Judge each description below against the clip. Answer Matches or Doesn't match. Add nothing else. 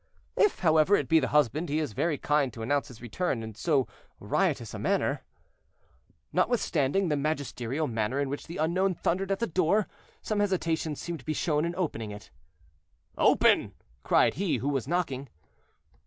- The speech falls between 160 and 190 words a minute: Matches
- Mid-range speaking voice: Matches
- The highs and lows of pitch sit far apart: Doesn't match